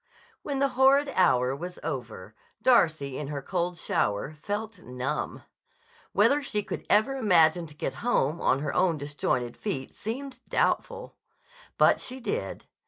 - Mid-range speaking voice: Yes, medium, 175 Hz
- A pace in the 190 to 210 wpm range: No, average, 145 wpm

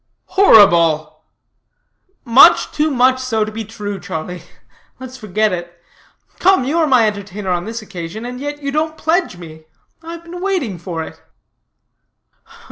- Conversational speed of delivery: Yes, average, 155 wpm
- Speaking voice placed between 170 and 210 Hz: No, high, 225 Hz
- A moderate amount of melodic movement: No, wide, 8.2 semitones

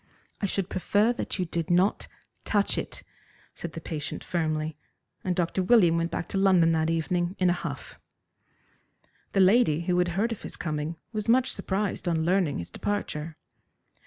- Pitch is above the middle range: No, medium, 175 Hz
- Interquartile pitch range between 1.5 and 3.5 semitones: Yes, average, 3.1 semitones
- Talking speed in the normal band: Yes, average, 170 wpm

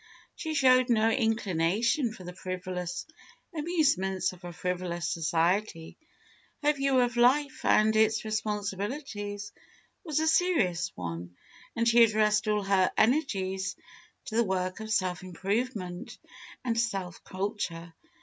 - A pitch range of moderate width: Yes, average, 4.5 semitones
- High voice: Yes, high, 205 Hz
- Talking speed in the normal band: No, slow, 125 wpm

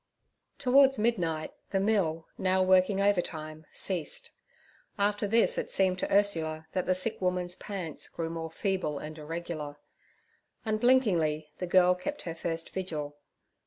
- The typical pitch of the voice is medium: Yes, medium, 180 Hz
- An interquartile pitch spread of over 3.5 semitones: Yes, average, 3.9 semitones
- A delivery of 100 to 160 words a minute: Yes, slow, 135 wpm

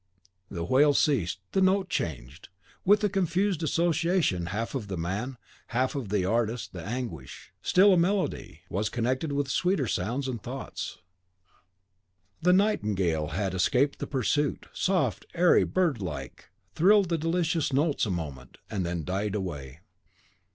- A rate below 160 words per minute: Yes, average, 145 wpm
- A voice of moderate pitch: No, low, 125 Hz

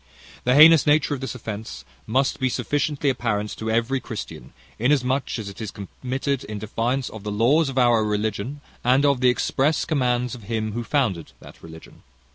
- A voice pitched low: Yes, low, 125 Hz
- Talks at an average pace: Yes, average, 180 wpm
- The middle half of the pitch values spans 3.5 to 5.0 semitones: Yes, average, 3.8 semitones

